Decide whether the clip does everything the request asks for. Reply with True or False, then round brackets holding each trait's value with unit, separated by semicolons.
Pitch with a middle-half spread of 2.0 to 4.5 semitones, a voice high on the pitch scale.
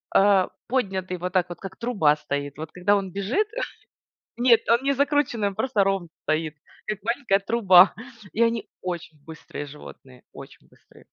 False (5.3 semitones; 195 Hz)